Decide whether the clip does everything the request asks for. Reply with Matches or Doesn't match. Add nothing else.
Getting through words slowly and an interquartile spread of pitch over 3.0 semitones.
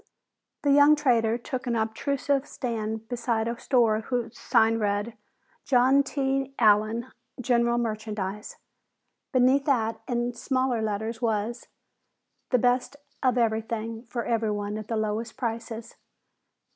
Doesn't match